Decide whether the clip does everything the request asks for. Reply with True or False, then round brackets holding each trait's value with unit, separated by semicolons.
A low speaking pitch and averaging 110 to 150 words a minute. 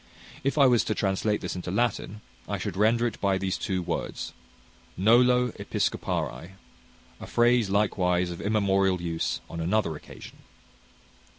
True (100 Hz; 140 wpm)